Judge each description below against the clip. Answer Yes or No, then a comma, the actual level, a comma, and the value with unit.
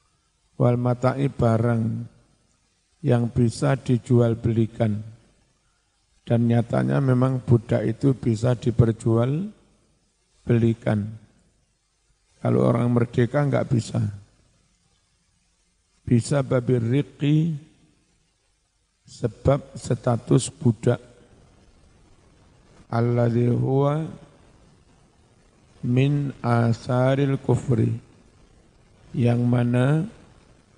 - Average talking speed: No, slow, 65 wpm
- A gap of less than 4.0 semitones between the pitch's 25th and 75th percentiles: Yes, narrow, 2.5 semitones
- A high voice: No, low, 120 Hz